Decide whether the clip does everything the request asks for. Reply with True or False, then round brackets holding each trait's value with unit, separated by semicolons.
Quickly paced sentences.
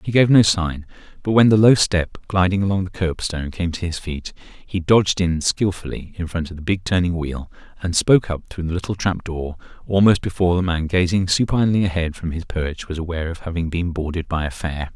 True (220 wpm)